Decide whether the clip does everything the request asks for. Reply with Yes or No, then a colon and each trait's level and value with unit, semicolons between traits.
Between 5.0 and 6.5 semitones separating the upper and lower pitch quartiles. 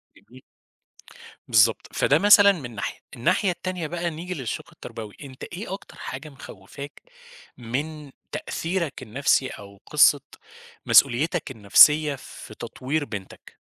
Yes: wide, 5.6 semitones